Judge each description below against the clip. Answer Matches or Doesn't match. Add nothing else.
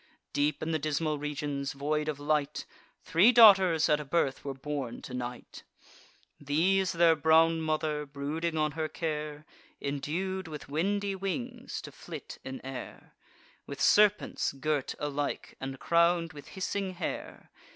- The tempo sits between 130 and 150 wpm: Matches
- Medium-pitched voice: Matches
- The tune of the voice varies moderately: Matches